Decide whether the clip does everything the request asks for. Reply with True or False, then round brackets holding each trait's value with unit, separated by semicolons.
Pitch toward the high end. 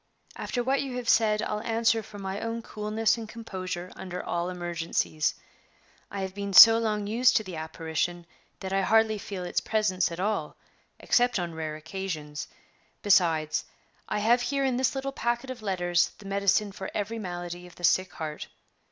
True (200 Hz)